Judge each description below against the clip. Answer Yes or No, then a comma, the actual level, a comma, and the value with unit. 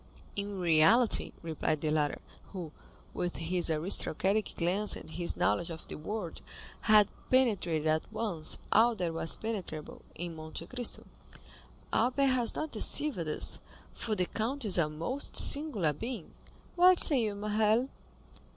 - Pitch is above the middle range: Yes, high, 200 Hz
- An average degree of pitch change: No, wide, 6.0 semitones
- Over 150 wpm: No, average, 140 wpm